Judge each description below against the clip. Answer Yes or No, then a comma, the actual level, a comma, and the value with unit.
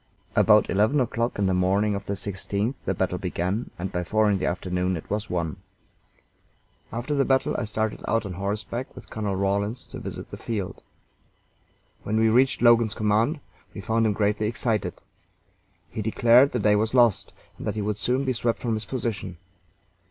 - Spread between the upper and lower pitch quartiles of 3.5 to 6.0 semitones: No, average, 2.9 semitones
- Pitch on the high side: No, low, 110 Hz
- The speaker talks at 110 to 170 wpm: No, average, 185 wpm